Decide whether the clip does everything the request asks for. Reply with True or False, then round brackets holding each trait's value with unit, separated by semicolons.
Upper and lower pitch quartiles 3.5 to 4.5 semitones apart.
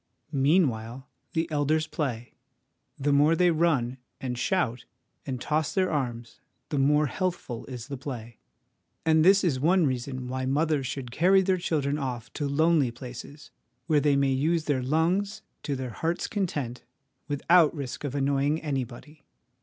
True (3.8 semitones)